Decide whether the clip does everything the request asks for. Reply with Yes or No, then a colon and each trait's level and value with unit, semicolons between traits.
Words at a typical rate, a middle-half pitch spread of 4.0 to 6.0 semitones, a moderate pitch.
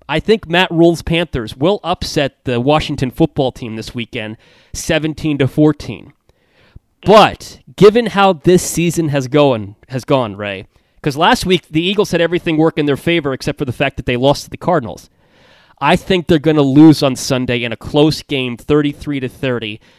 Yes: average, 185 wpm; average, 4.7 semitones; medium, 150 Hz